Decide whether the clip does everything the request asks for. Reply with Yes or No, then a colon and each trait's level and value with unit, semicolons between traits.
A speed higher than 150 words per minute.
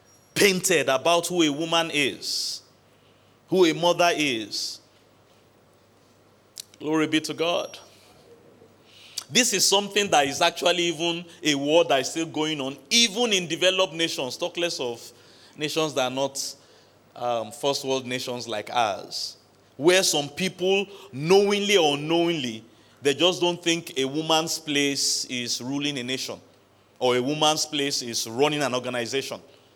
No: average, 140 wpm